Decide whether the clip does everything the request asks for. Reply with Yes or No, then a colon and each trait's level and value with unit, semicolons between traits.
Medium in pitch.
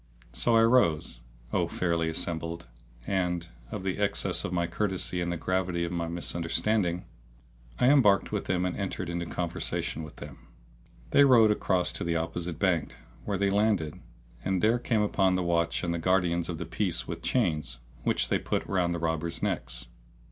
No: very low, 90 Hz